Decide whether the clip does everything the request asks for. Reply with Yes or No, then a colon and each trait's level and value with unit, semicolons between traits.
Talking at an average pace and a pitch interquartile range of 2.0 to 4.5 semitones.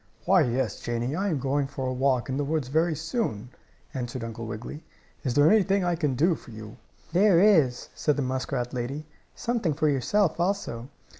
No: average, 190 wpm; average, 5.3 semitones